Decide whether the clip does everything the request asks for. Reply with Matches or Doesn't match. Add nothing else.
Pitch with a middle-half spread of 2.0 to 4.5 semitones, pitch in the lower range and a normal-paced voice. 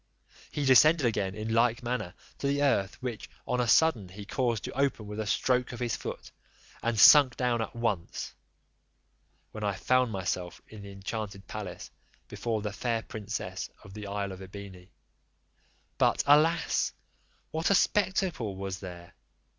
Matches